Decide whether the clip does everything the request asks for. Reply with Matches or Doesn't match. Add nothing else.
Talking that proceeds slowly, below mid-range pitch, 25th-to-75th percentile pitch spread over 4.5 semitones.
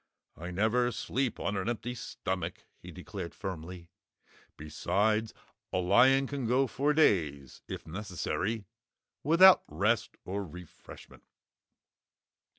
Matches